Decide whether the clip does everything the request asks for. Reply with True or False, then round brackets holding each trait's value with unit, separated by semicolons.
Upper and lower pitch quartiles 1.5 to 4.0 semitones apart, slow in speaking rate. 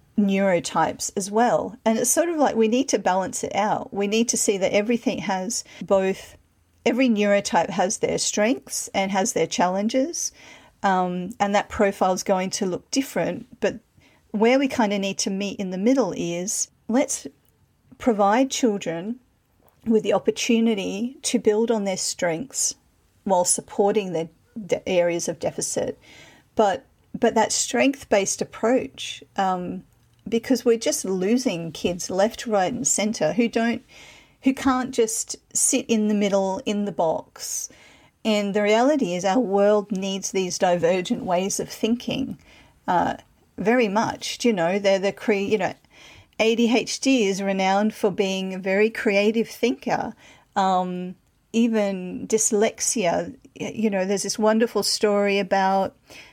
False (3.3 semitones; 150 wpm)